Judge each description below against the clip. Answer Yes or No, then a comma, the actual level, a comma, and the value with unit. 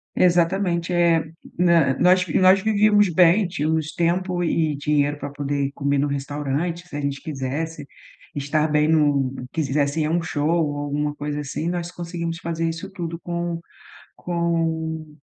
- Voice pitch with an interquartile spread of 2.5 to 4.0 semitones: Yes, average, 2.9 semitones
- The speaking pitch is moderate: Yes, medium, 160 Hz